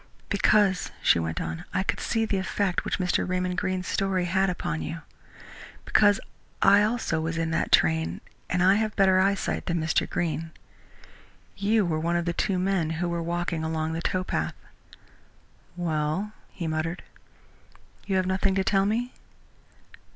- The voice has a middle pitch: Yes, medium, 180 Hz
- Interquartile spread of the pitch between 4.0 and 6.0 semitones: No, average, 3.0 semitones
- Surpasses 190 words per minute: No, average, 160 wpm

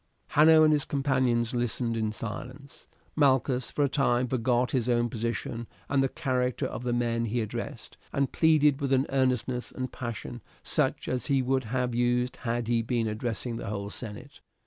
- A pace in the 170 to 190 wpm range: Yes, average, 175 wpm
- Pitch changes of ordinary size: No, narrow, 2.2 semitones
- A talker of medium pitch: No, low, 125 Hz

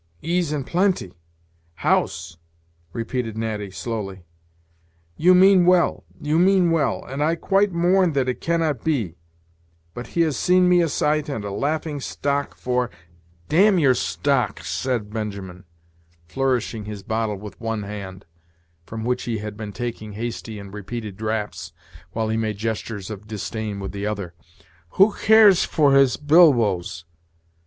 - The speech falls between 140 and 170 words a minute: Yes, average, 150 wpm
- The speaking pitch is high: No, low, 120 Hz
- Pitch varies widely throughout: Yes, wide, 7.0 semitones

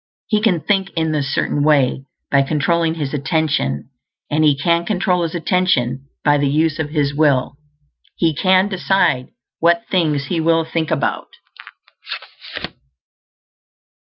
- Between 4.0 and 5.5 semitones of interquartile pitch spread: No, average, 3.3 semitones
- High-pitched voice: No, medium, 155 Hz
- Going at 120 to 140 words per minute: Yes, slow, 135 wpm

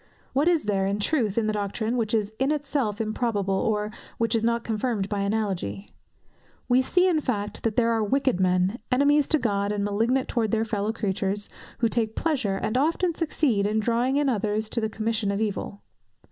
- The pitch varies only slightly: No, average, 3.6 semitones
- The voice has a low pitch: No, high, 220 Hz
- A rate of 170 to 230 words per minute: Yes, average, 195 wpm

